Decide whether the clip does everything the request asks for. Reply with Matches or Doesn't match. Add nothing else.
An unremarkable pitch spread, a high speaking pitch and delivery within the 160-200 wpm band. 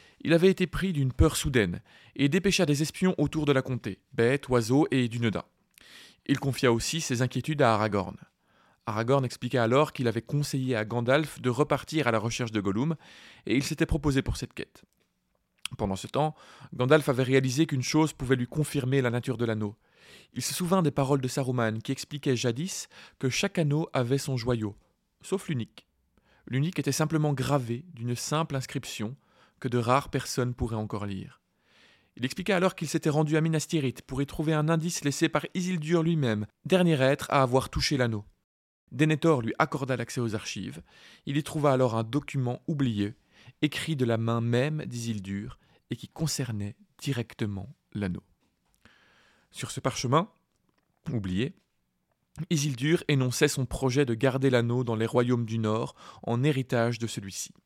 Doesn't match